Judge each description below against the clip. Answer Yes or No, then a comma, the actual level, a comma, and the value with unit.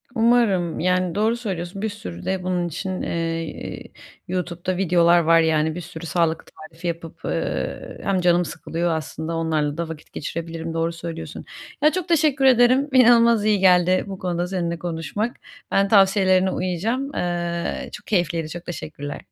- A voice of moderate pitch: Yes, medium, 175 Hz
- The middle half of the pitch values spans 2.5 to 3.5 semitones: Yes, average, 3.1 semitones